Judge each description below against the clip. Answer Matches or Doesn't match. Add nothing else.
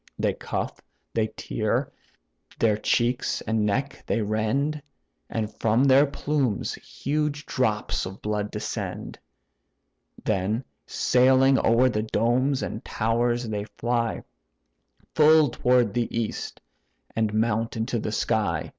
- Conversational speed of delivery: Doesn't match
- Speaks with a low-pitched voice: Matches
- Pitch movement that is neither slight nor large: Matches